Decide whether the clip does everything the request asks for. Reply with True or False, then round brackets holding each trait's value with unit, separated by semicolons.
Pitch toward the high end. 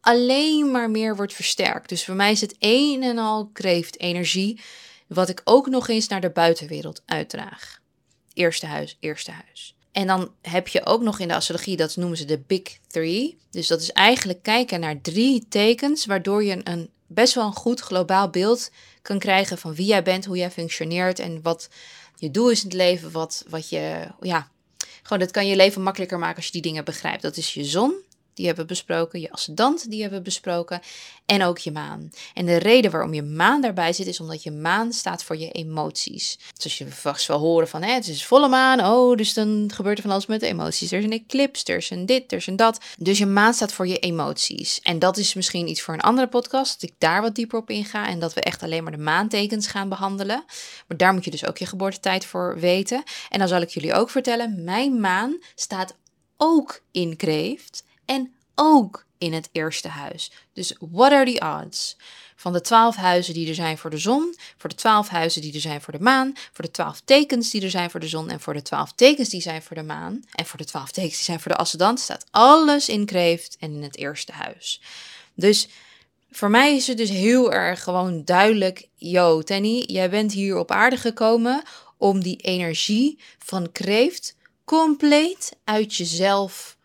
True (195 Hz)